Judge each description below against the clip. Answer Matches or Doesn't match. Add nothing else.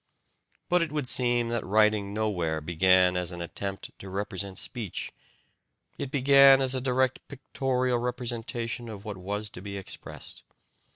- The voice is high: Doesn't match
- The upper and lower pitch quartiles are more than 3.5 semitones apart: Matches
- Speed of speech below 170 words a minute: Matches